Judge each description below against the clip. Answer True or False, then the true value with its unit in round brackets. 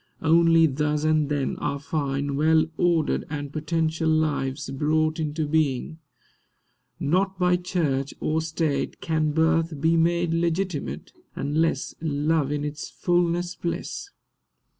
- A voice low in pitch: False (155 Hz)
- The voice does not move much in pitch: True (2.1 semitones)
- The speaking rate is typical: False (120 wpm)